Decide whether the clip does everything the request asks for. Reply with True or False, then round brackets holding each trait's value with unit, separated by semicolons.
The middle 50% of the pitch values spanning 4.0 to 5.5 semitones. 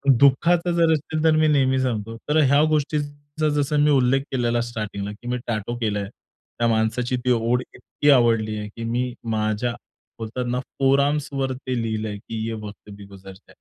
True (4.3 semitones)